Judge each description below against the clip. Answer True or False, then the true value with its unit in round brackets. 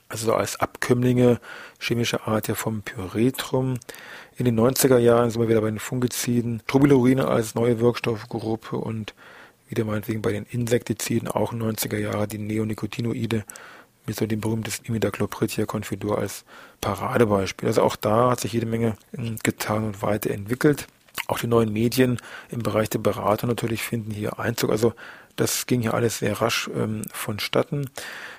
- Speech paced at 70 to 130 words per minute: False (155 wpm)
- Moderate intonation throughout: False (1.9 semitones)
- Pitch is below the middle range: True (115 Hz)